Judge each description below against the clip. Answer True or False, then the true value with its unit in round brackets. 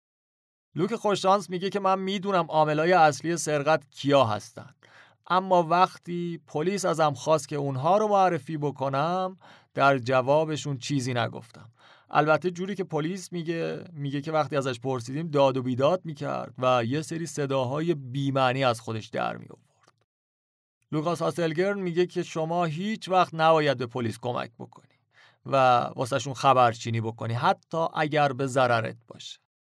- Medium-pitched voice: True (150 Hz)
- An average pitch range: True (4.7 semitones)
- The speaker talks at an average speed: True (140 wpm)